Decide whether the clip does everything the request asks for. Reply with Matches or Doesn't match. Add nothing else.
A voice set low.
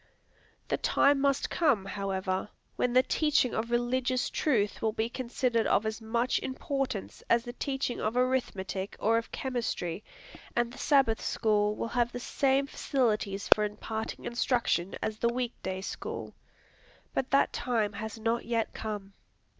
Doesn't match